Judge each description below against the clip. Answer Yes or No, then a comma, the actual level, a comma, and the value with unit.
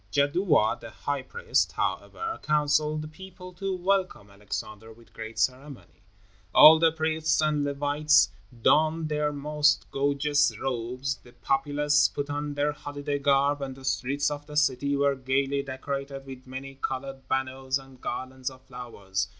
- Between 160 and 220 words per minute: No, average, 150 wpm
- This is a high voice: No, medium, 140 Hz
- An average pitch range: No, narrow, 2.3 semitones